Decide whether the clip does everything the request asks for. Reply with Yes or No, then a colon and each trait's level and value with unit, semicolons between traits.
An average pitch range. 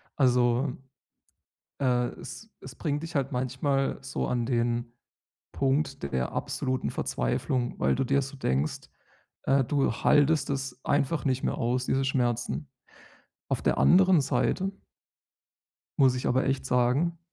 No: narrow, 2.2 semitones